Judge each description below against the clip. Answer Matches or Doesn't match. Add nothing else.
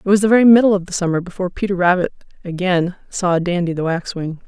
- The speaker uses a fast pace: Matches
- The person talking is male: Doesn't match